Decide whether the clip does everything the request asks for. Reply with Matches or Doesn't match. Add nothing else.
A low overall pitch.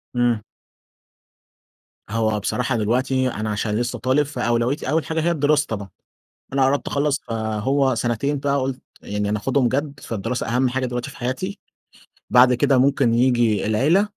Matches